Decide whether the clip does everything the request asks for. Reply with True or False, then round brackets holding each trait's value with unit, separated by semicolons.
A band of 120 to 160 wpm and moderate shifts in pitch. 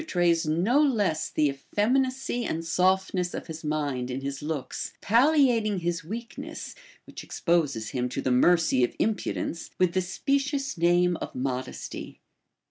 False (155 wpm; 6.8 semitones)